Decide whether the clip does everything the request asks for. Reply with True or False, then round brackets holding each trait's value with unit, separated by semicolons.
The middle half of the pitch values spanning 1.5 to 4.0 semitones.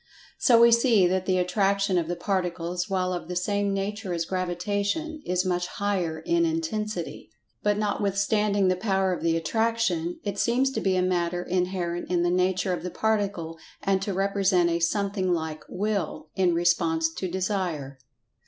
True (2.6 semitones)